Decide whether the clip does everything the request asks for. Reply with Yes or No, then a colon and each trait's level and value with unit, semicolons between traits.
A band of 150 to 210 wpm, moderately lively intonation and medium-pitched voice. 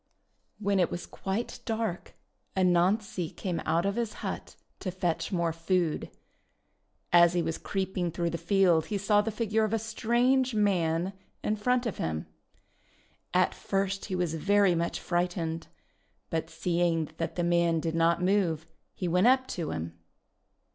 Yes: average, 155 wpm; average, 3.5 semitones; medium, 180 Hz